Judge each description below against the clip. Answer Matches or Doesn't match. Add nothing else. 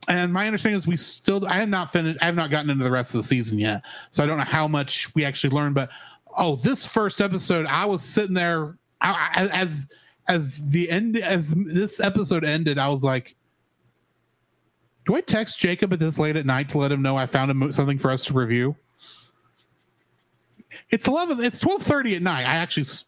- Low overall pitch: Doesn't match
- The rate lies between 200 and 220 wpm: Matches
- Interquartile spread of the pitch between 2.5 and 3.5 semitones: Doesn't match